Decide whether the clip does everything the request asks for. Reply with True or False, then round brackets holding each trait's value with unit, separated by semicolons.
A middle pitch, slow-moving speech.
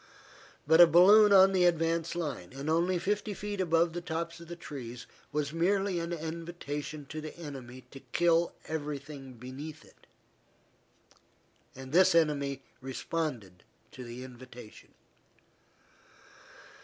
True (160 Hz; 130 wpm)